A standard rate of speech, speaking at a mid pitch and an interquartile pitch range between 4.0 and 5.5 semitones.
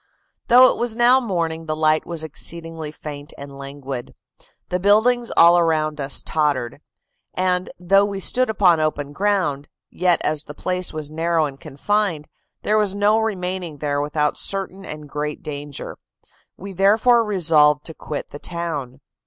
Yes: average, 155 wpm; medium, 165 Hz; average, 4.8 semitones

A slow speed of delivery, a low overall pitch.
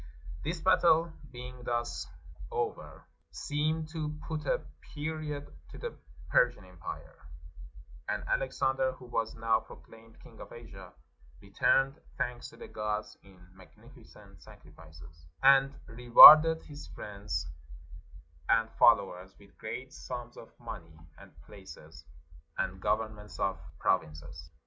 Yes: slow, 120 wpm; low, 120 Hz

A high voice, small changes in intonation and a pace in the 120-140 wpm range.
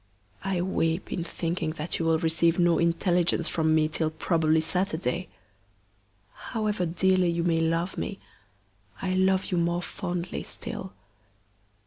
No: medium, 170 Hz; narrow, 2.0 semitones; slow, 135 wpm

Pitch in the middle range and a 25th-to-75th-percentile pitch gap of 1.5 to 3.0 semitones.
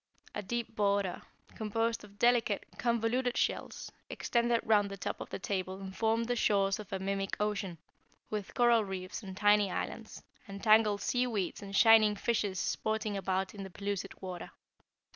No: high, 205 Hz; narrow, 2.5 semitones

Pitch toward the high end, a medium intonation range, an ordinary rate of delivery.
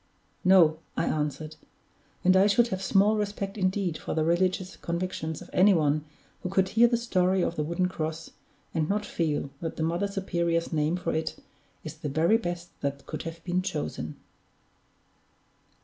No: medium, 175 Hz; average, 3.2 semitones; average, 170 wpm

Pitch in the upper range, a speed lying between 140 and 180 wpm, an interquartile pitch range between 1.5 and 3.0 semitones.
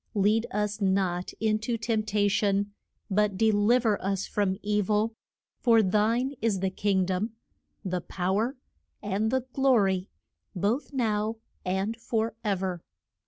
Yes: high, 210 Hz; average, 160 wpm; narrow, 2.5 semitones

